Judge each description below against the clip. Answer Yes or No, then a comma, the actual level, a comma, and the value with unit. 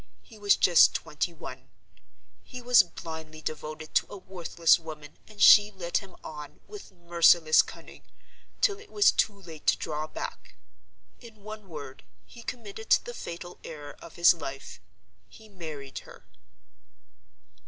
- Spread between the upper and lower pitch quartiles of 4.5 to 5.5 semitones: Yes, average, 5.0 semitones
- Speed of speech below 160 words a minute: Yes, average, 145 wpm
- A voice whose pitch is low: No, medium, 175 Hz